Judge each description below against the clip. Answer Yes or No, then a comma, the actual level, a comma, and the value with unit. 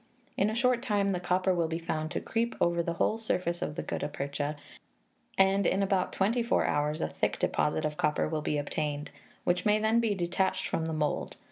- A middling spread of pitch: Yes, average, 4.7 semitones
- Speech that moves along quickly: Yes, fast, 215 wpm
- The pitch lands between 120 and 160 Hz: No, medium, 175 Hz